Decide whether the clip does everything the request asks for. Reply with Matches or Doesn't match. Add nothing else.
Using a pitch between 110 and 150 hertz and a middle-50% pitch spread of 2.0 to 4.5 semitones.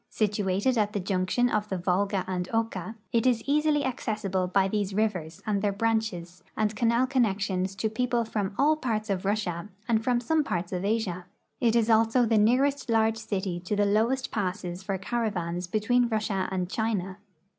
Doesn't match